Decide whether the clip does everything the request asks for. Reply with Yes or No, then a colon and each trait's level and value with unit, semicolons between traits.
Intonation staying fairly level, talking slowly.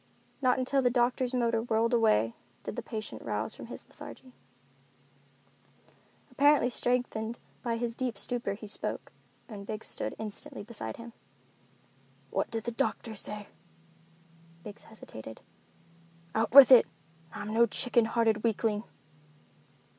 Yes: narrow, 2.3 semitones; slow, 130 wpm